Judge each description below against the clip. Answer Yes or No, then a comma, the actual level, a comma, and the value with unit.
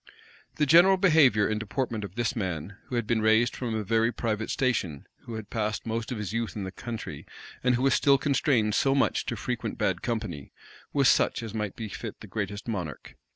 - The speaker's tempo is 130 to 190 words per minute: No, fast, 205 wpm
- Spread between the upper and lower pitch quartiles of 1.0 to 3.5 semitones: Yes, average, 2.9 semitones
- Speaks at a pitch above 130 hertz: No, low, 115 Hz